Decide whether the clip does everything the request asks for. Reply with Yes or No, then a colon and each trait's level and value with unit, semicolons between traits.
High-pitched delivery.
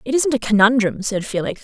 Yes: high, 230 Hz